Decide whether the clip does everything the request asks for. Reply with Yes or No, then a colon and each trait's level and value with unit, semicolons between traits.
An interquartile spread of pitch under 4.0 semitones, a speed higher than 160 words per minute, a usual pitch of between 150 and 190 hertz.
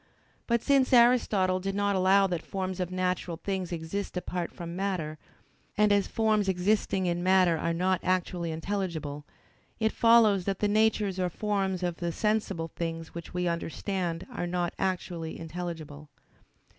No: average, 2.8 semitones; average, 155 wpm; medium, 185 Hz